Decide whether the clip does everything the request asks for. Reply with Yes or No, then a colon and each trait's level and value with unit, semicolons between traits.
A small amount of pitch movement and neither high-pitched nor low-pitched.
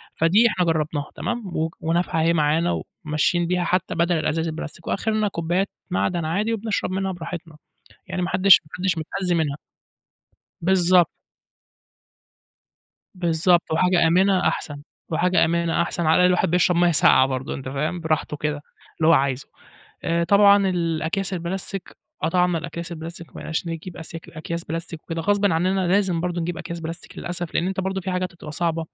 Yes: narrow, 2.1 semitones; medium, 170 Hz